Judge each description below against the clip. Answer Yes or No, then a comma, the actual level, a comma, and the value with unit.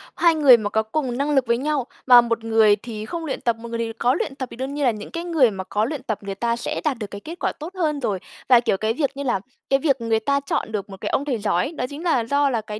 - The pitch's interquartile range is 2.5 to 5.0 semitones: Yes, average, 4.3 semitones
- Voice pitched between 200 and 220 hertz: No, high, 245 Hz